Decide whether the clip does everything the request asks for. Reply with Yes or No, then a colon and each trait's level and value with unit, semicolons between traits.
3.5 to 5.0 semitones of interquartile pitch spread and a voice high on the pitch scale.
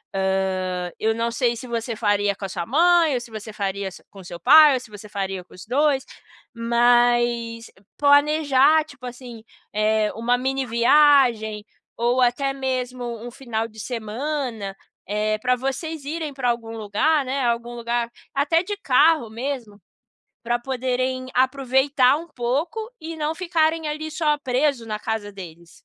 Yes: average, 4.3 semitones; high, 245 Hz